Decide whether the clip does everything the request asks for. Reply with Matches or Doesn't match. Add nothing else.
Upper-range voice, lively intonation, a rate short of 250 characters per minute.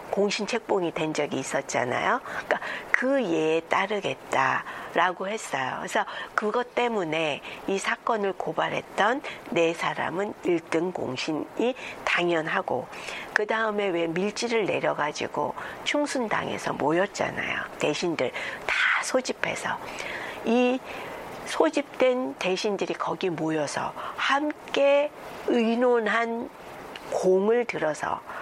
Matches